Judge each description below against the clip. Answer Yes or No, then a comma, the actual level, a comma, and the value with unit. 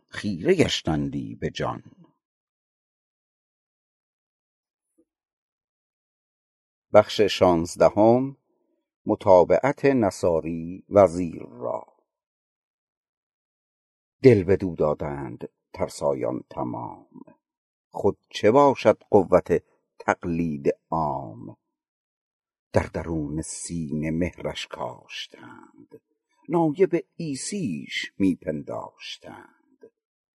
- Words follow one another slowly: Yes, slow, 55 wpm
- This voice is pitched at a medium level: No, very low, 90 Hz